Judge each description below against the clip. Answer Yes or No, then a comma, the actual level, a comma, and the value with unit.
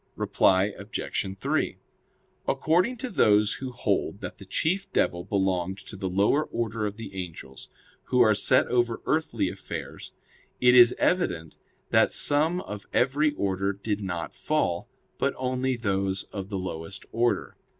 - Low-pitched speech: Yes, low, 105 Hz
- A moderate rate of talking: Yes, average, 150 wpm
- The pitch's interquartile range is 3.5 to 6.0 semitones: Yes, average, 5.1 semitones